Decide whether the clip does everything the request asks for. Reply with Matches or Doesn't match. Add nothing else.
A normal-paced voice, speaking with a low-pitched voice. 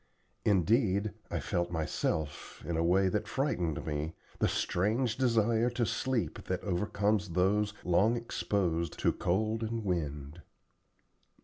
Doesn't match